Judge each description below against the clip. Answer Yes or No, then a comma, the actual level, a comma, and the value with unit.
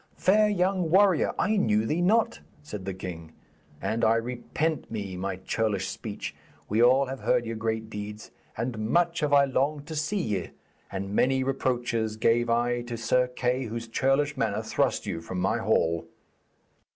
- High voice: No, low, 120 Hz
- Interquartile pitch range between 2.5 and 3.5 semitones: No, average, 4.9 semitones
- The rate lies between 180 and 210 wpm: No, average, 170 wpm